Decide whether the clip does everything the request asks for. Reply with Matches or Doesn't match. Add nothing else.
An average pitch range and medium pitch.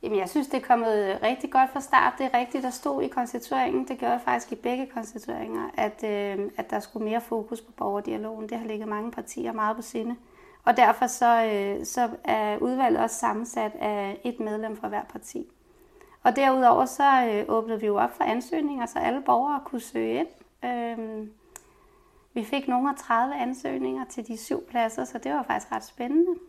Doesn't match